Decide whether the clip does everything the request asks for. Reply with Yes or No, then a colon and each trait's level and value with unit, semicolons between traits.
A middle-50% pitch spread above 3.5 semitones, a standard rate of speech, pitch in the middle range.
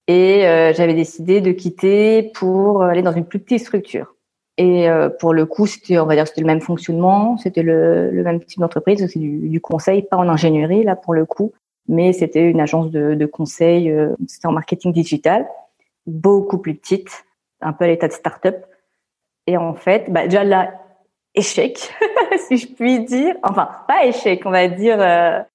No: average, 3.2 semitones; average, 195 wpm; medium, 180 Hz